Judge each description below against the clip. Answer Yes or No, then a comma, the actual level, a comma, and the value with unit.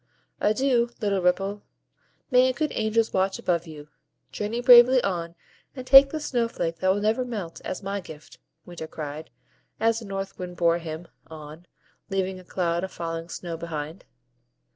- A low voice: No, high, 190 Hz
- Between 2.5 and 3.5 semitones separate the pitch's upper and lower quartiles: No, average, 5.2 semitones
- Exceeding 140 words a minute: Yes, average, 165 wpm